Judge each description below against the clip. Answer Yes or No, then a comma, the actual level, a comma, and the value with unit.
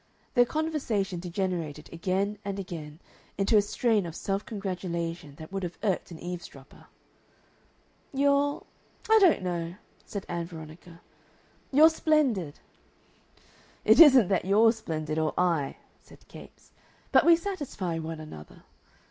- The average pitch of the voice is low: No, medium, 185 Hz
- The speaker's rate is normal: No, slow, 130 wpm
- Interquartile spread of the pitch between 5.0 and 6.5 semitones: Yes, wide, 5.5 semitones